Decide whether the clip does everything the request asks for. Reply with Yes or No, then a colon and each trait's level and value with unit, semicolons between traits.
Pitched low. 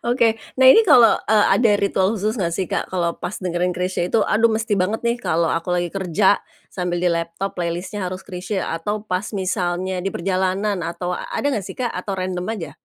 No: medium, 185 Hz